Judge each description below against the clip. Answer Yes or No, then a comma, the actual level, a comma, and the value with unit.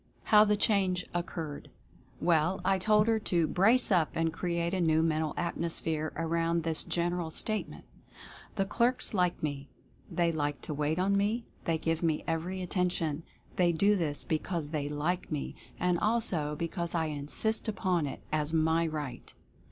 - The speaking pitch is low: No, medium, 170 Hz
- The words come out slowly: No, average, 160 wpm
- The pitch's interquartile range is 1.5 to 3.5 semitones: Yes, average, 3.0 semitones